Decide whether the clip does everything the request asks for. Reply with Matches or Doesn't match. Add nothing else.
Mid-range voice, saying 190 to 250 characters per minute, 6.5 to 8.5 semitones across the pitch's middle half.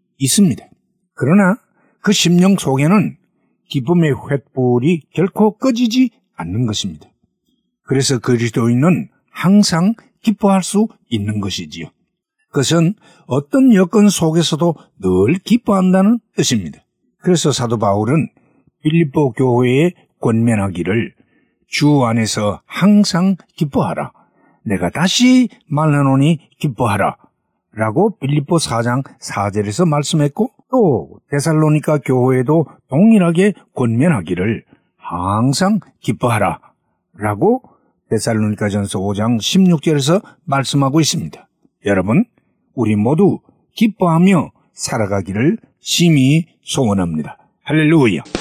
Matches